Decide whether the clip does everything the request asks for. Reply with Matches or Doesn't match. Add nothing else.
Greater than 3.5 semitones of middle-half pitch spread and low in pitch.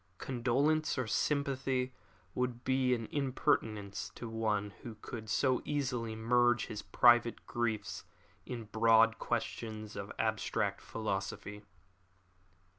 Doesn't match